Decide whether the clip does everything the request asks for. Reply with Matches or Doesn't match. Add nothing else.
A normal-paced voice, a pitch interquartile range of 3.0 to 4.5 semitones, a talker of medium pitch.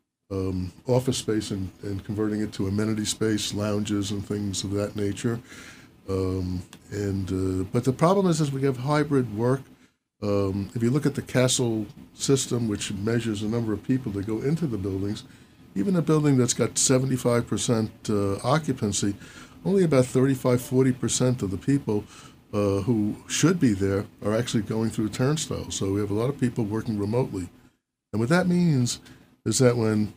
Doesn't match